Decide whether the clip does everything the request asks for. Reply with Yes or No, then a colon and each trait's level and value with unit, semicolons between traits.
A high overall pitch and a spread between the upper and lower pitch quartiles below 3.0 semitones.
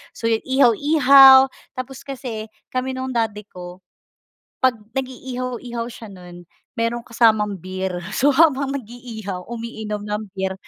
No: high, 235 Hz; average, 3.8 semitones